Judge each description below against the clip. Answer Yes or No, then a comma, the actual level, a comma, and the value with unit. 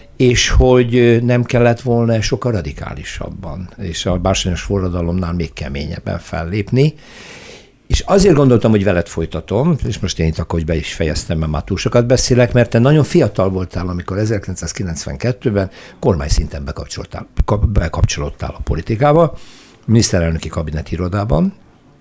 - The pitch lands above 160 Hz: No, low, 100 Hz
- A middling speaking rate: Yes, average, 135 wpm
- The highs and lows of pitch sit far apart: Yes, wide, 6.0 semitones